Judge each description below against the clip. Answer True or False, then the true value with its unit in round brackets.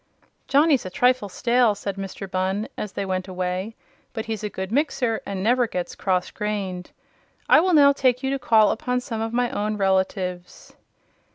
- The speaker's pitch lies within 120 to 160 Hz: False (210 Hz)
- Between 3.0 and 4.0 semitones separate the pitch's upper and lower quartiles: False (4.6 semitones)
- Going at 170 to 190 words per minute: True (180 wpm)